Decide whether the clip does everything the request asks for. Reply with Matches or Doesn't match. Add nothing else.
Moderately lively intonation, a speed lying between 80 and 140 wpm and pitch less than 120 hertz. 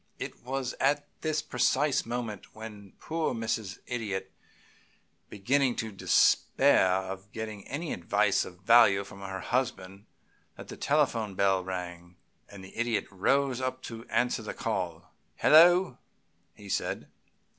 Matches